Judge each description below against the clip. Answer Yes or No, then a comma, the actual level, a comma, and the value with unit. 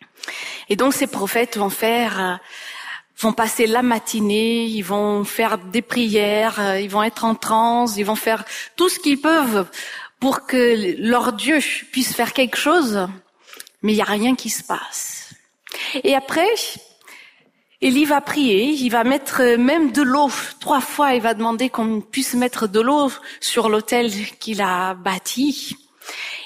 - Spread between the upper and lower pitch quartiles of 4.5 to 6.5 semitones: No, average, 3.9 semitones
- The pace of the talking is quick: No, average, 155 wpm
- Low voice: No, high, 235 Hz